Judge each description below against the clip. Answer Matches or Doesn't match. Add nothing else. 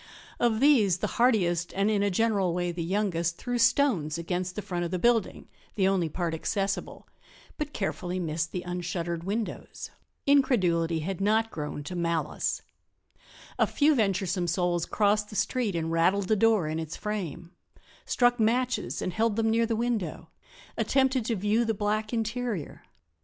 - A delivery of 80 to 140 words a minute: Doesn't match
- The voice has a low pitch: Doesn't match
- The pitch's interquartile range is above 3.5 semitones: Matches